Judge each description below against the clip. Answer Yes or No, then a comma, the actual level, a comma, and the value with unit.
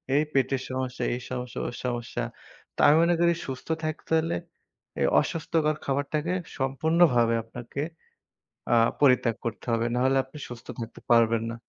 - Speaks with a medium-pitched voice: No, low, 130 Hz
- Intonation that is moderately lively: Yes, average, 4.0 semitones